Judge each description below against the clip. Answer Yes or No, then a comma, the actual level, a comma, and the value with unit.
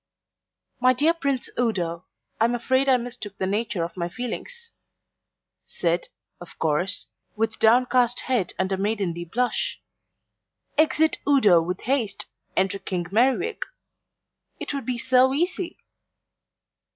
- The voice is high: Yes, high, 235 Hz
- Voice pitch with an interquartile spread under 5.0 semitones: No, wide, 5.6 semitones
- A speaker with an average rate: No, slow, 125 wpm